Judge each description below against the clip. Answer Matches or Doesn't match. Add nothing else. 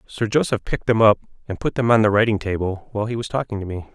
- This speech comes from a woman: Doesn't match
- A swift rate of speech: Matches